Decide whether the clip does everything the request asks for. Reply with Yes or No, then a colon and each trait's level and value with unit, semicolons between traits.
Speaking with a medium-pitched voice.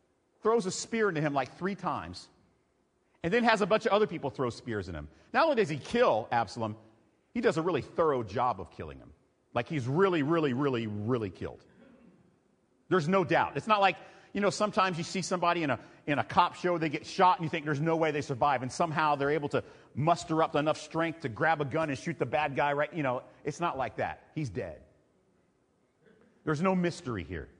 Yes: medium, 160 Hz